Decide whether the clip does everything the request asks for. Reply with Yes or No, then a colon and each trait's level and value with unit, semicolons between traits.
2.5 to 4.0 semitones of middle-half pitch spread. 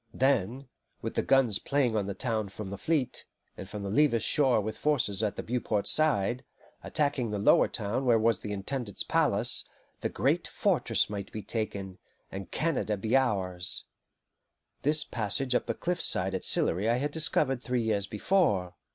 No: average, 5.0 semitones